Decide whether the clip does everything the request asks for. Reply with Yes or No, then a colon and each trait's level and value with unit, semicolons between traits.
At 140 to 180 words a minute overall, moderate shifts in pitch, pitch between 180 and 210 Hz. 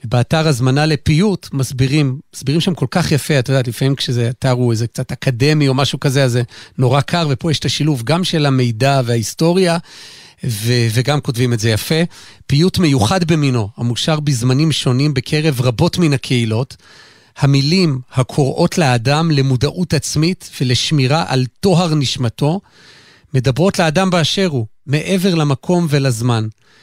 No: average, 145 wpm; average, 4.0 semitones; medium, 140 Hz